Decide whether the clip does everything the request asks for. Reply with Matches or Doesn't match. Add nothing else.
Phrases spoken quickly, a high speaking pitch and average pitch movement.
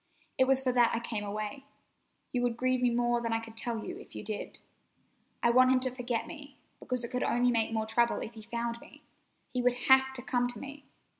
Doesn't match